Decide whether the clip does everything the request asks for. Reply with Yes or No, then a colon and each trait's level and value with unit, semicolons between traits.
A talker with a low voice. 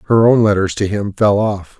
Yes: low, 105 Hz